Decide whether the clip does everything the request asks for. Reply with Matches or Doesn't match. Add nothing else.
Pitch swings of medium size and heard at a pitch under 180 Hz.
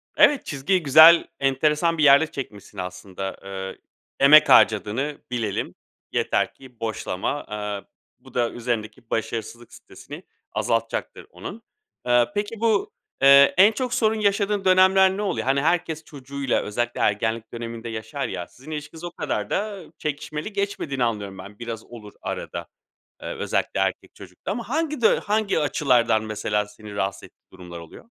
Doesn't match